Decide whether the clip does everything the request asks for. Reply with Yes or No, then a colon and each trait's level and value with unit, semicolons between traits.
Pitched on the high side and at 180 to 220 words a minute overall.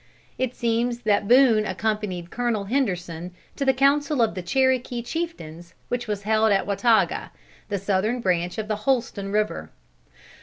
No: high, 215 Hz; average, 150 wpm